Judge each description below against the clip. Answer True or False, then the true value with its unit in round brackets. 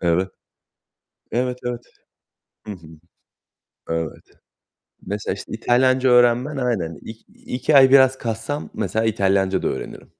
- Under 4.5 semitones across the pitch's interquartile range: False (4.8 semitones)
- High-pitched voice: False (115 Hz)